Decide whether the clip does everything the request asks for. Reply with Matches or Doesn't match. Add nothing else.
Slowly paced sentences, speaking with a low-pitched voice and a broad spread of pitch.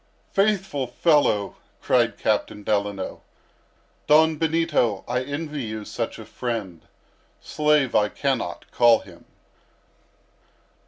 Matches